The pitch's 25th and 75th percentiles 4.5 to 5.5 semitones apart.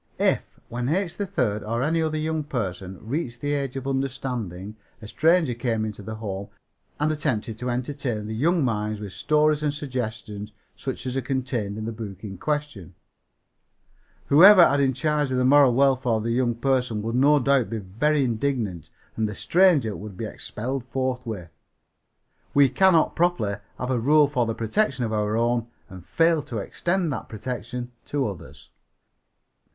Yes: average, 5.0 semitones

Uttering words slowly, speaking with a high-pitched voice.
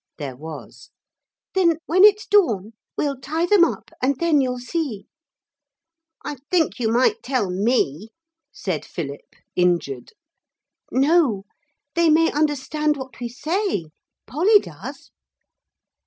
Yes: slow, 120 wpm; very high, 275 Hz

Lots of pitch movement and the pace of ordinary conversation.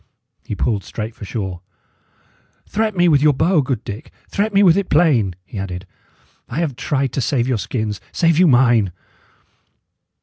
Yes: wide, 7.6 semitones; average, 170 wpm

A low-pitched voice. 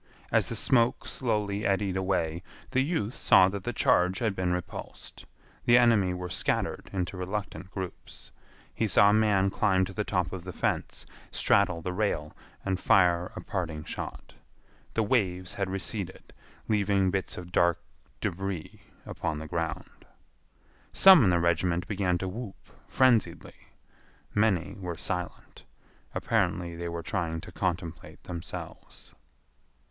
Yes: very low, 95 Hz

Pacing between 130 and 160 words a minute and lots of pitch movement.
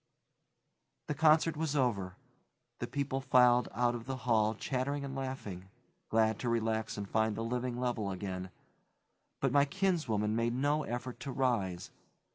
No: average, 150 wpm; average, 3.7 semitones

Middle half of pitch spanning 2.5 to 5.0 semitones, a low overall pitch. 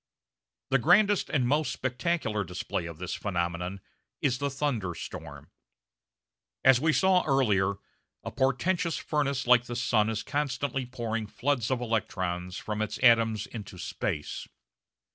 No: wide, 5.4 semitones; low, 120 Hz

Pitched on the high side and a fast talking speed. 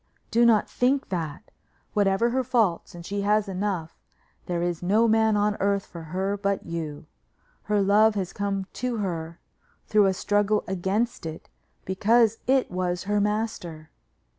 No: high, 200 Hz; average, 155 wpm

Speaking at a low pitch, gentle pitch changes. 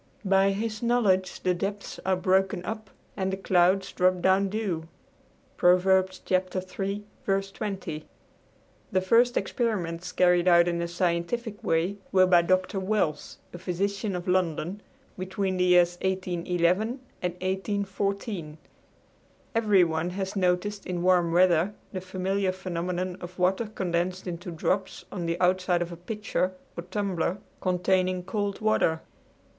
No: medium, 185 Hz; narrow, 1.9 semitones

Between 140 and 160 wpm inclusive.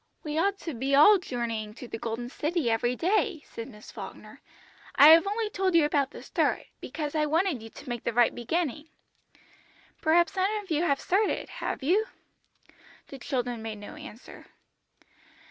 No: average, 175 wpm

